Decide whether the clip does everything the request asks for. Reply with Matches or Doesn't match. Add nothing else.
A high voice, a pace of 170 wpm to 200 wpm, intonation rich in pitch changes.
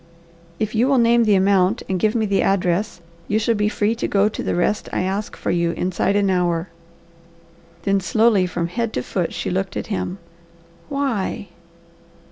Doesn't match